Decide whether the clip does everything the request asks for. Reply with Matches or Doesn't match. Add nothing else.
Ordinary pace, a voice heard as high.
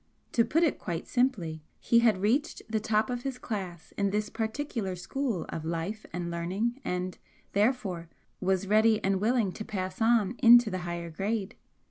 Matches